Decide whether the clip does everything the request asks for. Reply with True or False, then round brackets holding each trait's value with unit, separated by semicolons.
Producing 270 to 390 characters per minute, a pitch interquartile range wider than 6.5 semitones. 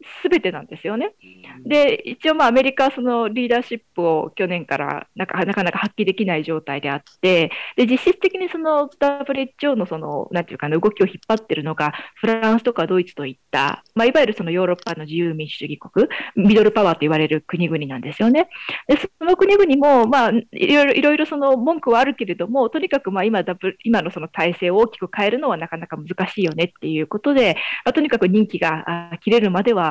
False (425 characters per minute; 7.8 semitones)